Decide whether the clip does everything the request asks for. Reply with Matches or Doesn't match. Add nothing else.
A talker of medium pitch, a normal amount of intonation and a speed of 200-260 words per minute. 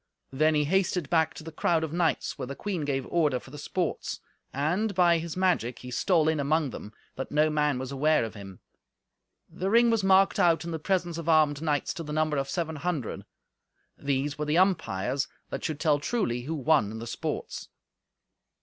Matches